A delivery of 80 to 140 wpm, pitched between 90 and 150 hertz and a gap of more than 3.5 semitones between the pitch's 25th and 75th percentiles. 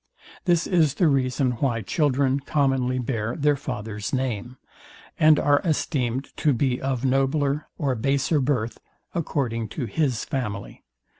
No: slow, 135 wpm; low, 135 Hz; average, 3.0 semitones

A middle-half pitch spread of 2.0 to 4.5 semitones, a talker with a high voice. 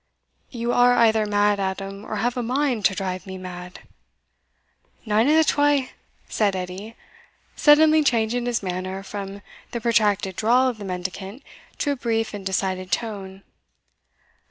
Yes: average, 4.1 semitones; high, 210 Hz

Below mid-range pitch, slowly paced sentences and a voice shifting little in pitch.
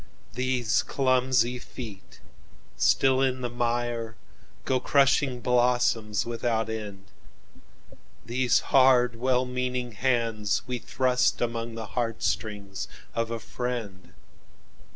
Yes: low, 120 Hz; slow, 90 wpm; narrow, 2.1 semitones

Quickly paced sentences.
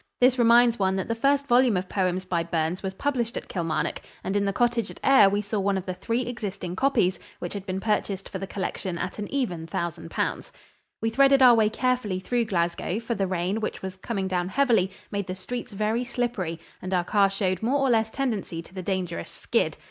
Yes: fast, 220 wpm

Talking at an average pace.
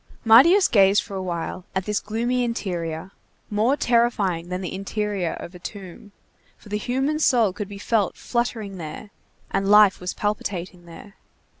Yes: average, 160 wpm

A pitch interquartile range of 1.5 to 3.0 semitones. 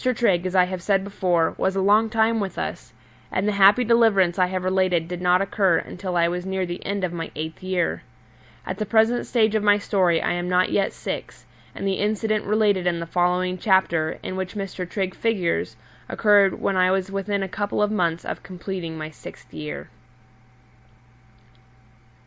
Yes: narrow, 2.4 semitones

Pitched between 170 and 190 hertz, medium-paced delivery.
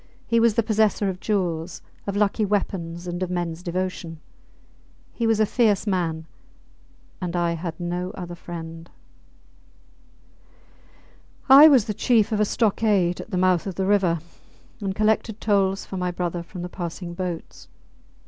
Yes: medium, 185 Hz; average, 155 wpm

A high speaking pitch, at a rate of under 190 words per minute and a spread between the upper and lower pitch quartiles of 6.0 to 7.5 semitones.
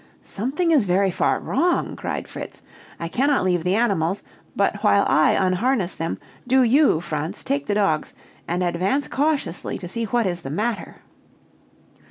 Yes: high, 195 Hz; average, 160 wpm; wide, 6.8 semitones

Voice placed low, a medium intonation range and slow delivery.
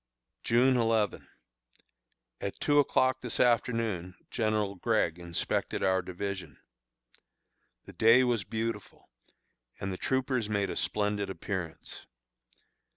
Yes: low, 105 Hz; average, 3.5 semitones; slow, 105 wpm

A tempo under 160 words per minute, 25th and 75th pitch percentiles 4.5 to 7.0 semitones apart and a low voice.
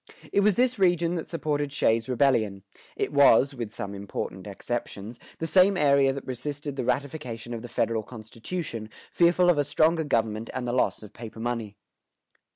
No: average, 175 wpm; wide, 5.5 semitones; low, 130 Hz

